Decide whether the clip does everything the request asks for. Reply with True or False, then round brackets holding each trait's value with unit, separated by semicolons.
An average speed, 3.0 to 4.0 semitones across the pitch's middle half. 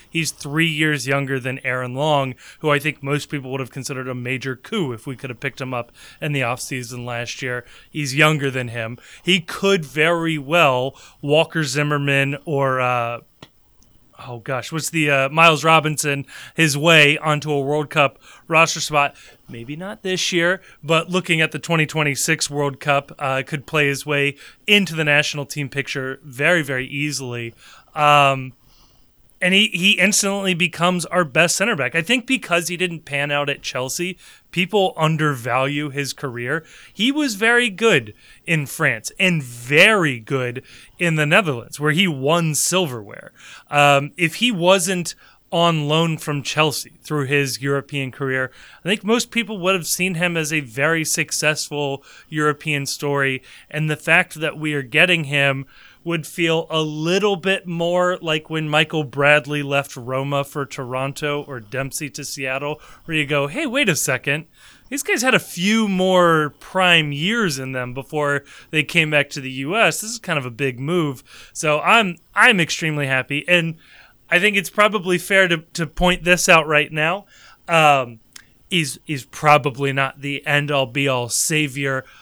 True (170 wpm; 3.7 semitones)